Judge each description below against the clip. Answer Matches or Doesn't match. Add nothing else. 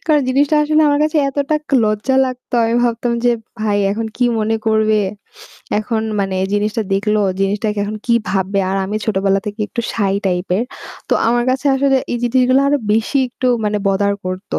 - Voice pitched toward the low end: Doesn't match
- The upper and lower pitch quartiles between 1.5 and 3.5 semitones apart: Doesn't match